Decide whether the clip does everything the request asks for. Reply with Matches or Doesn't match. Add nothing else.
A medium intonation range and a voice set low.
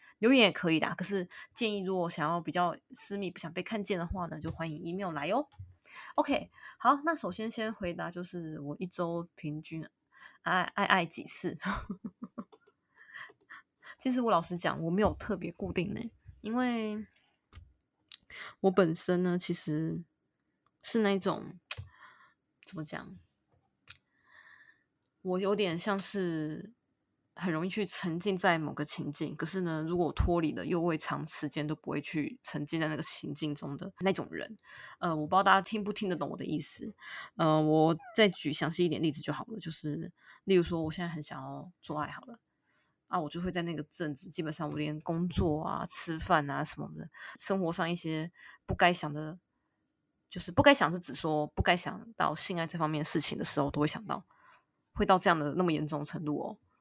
Doesn't match